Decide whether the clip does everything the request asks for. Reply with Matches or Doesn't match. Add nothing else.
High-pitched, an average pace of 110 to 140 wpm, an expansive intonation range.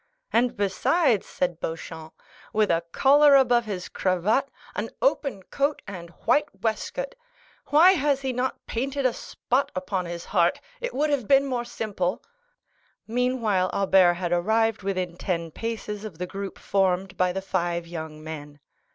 Doesn't match